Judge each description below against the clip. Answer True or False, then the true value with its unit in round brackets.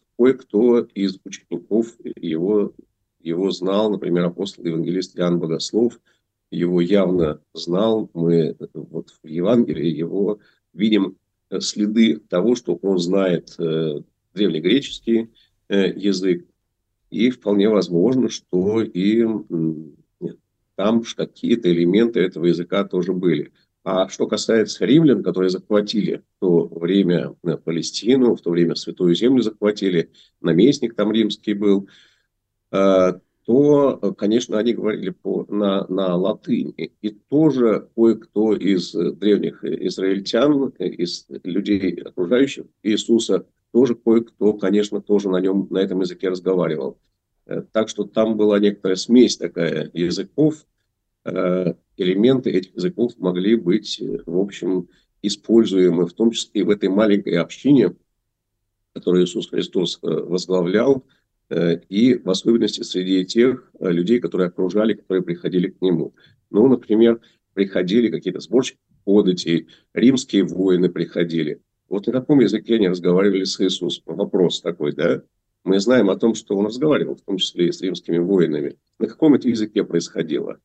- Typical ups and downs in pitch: True (3.5 semitones)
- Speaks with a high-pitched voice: False (100 Hz)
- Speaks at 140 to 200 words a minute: False (125 wpm)